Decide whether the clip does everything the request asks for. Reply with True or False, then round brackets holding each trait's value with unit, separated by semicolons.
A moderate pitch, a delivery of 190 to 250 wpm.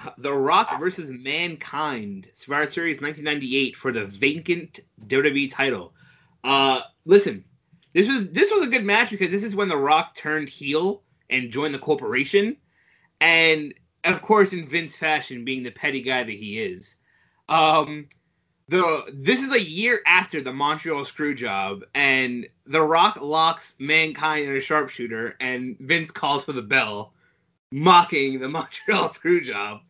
False (155 Hz; 150 wpm)